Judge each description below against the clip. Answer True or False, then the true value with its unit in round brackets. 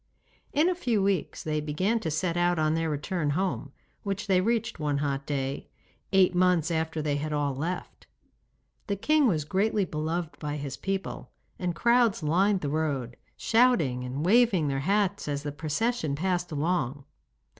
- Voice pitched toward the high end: False (165 Hz)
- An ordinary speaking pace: True (165 wpm)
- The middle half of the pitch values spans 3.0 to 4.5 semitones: False (5.0 semitones)